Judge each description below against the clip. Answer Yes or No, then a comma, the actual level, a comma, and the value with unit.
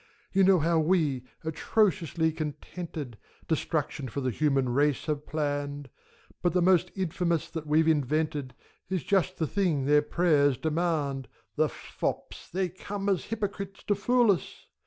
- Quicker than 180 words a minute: No, average, 145 wpm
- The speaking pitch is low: No, medium, 160 Hz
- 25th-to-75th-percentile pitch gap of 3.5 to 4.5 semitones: Yes, average, 4.0 semitones